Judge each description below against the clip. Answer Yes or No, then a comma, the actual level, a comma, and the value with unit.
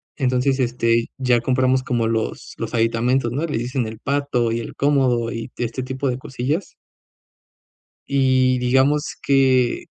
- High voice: No, low, 125 Hz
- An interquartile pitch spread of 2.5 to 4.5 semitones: No, narrow, 2.1 semitones